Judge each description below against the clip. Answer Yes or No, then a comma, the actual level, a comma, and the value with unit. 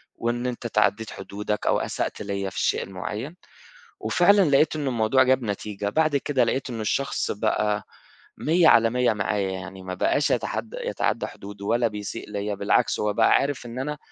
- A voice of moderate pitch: No, low, 110 Hz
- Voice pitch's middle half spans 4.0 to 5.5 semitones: Yes, average, 4.3 semitones